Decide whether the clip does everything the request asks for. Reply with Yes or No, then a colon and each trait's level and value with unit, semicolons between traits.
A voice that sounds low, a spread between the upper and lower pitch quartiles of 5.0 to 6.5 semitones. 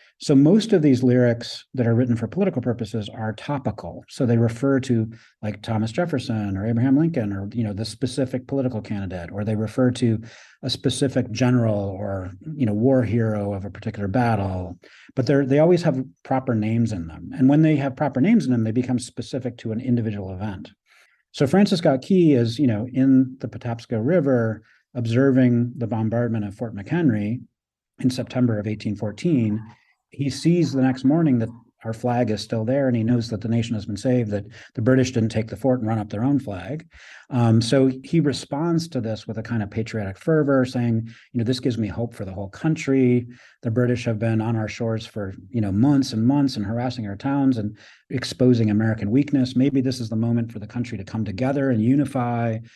No: low, 120 Hz; average, 3.1 semitones